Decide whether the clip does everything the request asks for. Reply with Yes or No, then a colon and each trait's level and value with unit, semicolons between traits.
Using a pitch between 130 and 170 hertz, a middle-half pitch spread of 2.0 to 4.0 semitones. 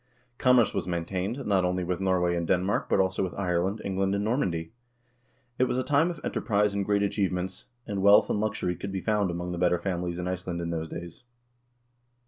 No: very low, 95 Hz; narrow, 2.4 semitones